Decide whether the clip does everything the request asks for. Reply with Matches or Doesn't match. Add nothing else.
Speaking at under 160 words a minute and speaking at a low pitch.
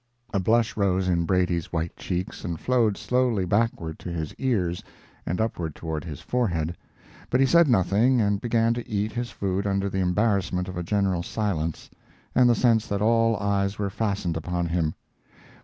Doesn't match